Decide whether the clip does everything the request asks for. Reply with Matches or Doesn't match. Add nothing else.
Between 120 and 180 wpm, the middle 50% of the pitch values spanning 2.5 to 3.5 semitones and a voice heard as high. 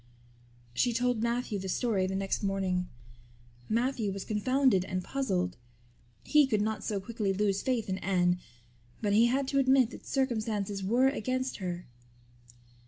Doesn't match